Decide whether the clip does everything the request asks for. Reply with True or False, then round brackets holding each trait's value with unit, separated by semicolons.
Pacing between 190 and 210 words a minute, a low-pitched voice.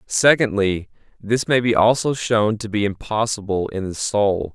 False (160 wpm; 105 Hz)